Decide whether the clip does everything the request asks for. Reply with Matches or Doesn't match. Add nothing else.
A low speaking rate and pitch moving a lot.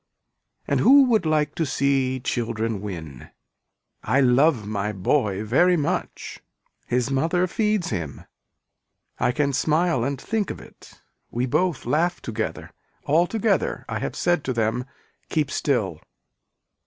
Matches